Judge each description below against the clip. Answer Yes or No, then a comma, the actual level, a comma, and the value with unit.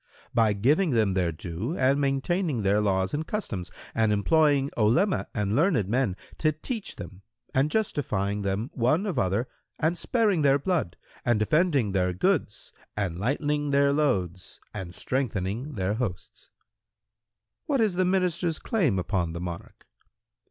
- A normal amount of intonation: No, wide, 7.9 semitones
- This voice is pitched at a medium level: No, low, 125 Hz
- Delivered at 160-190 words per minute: No, average, 150 wpm